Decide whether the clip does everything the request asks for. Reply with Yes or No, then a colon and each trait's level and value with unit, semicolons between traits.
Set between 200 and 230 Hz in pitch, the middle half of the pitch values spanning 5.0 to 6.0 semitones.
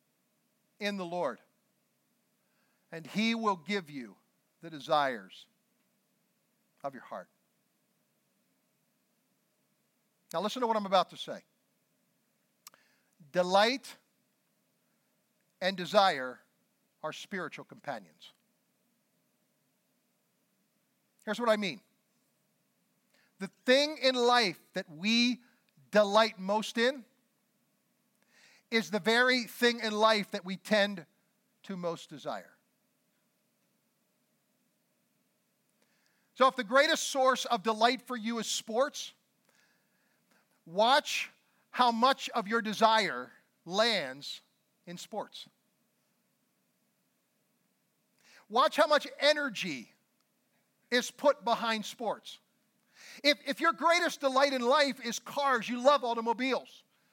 No: high, 220 Hz; average, 3.4 semitones